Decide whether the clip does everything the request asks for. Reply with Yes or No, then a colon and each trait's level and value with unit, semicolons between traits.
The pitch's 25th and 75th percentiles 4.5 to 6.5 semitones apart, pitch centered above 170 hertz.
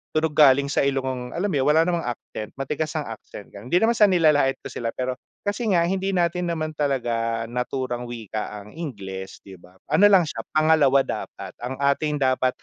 No: average, 4.9 semitones; medium, 140 Hz